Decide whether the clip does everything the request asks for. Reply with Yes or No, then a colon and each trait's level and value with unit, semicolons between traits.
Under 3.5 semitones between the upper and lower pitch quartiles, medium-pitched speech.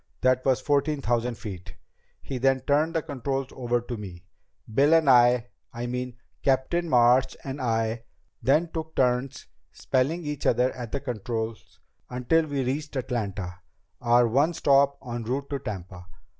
No: average, 2.9 semitones; low, 130 Hz